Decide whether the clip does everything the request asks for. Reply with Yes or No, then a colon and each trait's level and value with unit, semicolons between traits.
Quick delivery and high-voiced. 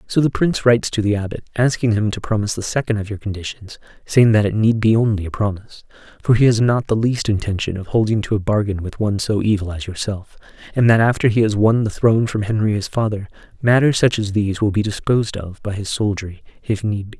No: fast, 235 wpm; low, 105 Hz